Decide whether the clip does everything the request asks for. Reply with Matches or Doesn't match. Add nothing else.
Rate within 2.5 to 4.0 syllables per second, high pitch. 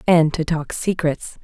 Doesn't match